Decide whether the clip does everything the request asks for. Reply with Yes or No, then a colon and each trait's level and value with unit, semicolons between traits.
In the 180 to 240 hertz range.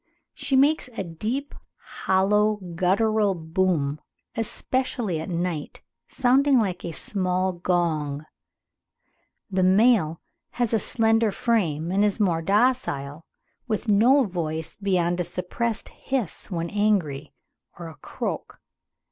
Yes: high, 190 Hz